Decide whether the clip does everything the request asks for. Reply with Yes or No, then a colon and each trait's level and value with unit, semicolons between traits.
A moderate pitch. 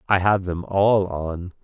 No: very low, 95 Hz